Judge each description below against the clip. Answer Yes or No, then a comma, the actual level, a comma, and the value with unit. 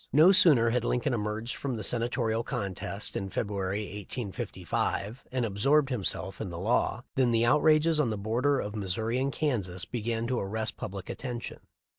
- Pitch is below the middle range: Yes, low, 115 Hz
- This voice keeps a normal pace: Yes, average, 170 wpm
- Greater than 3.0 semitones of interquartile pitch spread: Yes, average, 3.8 semitones